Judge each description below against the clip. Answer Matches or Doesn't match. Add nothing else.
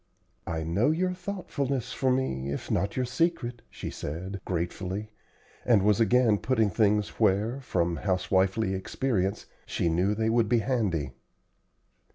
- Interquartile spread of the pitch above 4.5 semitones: Matches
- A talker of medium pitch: Doesn't match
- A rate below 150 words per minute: Matches